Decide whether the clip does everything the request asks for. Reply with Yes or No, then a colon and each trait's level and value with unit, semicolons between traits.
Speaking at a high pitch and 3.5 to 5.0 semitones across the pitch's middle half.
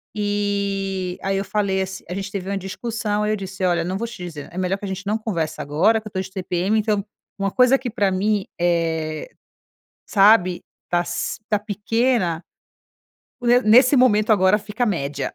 No: high, 195 Hz; average, 2.7 semitones